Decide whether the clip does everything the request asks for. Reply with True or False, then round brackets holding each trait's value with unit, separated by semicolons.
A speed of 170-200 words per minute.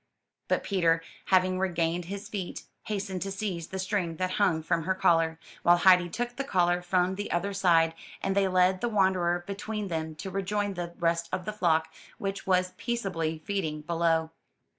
True (180 wpm)